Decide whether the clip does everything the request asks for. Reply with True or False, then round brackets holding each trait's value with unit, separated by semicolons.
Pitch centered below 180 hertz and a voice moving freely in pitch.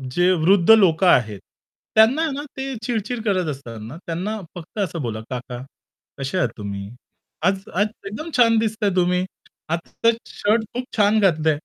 False (185 Hz; 5.7 semitones)